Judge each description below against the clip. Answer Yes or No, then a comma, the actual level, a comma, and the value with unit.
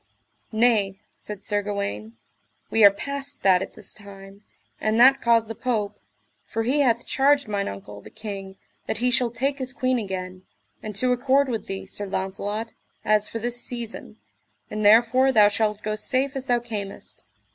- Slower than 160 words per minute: No, average, 175 wpm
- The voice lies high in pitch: Yes, high, 220 Hz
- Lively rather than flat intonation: No, average, 3.7 semitones